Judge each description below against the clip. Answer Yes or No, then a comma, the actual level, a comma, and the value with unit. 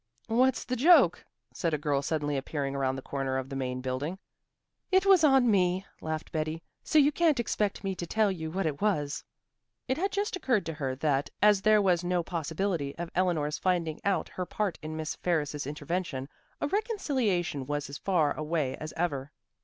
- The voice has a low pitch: No, medium, 170 Hz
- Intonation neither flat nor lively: No, wide, 6.1 semitones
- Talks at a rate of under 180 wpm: No, average, 190 wpm